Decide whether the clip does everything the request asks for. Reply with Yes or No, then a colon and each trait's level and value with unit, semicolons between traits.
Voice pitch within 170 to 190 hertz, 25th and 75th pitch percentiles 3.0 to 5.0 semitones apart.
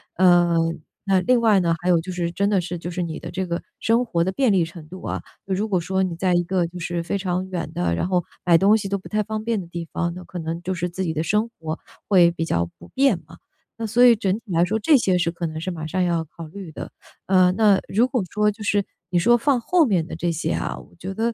Yes: medium, 185 Hz; average, 3.5 semitones